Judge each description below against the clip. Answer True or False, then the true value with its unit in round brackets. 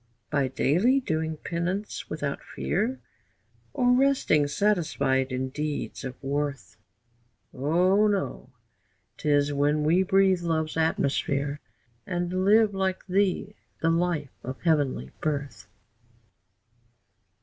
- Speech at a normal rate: False (105 wpm)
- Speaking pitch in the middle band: True (160 Hz)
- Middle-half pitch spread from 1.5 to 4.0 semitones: False (4.9 semitones)